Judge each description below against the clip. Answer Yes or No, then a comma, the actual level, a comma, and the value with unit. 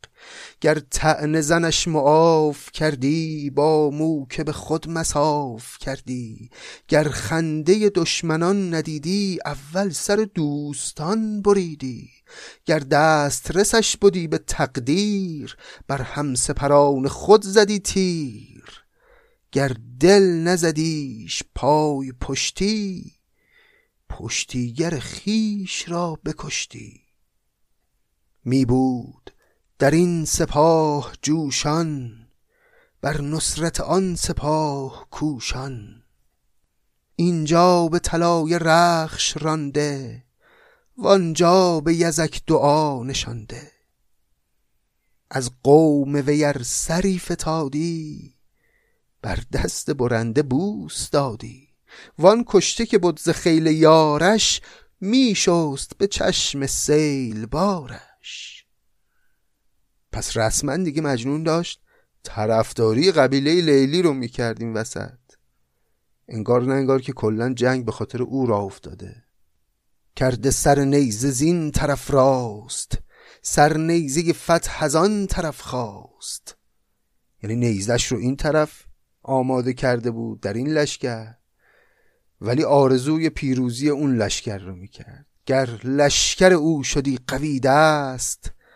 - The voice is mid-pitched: Yes, medium, 150 Hz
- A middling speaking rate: No, slow, 95 wpm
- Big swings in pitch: No, average, 4.8 semitones